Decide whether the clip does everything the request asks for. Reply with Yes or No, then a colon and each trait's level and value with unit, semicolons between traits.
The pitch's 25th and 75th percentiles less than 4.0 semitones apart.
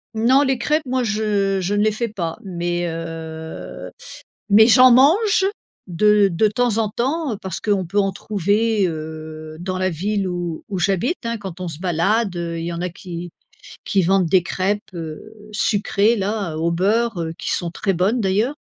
No: average, 4.3 semitones